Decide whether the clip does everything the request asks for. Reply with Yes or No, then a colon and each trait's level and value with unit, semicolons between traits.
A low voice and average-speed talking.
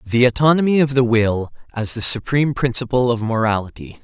Yes: low, 125 Hz; average, 165 wpm